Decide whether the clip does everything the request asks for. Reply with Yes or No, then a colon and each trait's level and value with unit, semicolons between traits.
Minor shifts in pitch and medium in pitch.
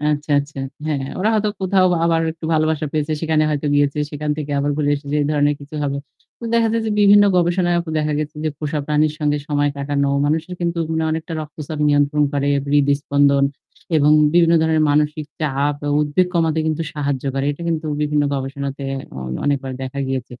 Yes: narrow, 2.0 semitones; medium, 150 Hz